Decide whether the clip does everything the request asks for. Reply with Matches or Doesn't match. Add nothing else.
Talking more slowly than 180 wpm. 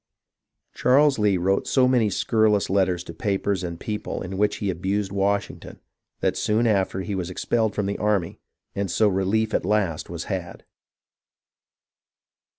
Matches